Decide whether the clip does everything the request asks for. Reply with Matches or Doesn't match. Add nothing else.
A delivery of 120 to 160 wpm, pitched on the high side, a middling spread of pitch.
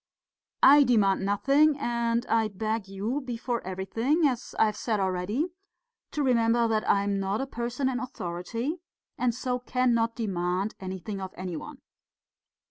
Matches